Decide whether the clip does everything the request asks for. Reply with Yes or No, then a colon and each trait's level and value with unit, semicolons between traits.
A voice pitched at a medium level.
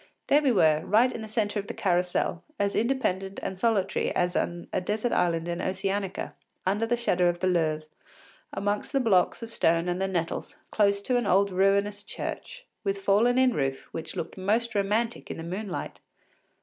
No: high, 195 Hz